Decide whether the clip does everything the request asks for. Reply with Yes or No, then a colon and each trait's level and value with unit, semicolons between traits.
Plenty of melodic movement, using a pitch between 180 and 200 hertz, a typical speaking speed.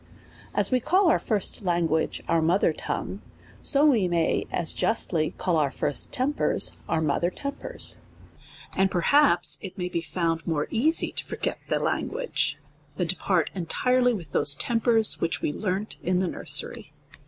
Yes: wide, 6.3 semitones; medium, 185 Hz; average, 170 wpm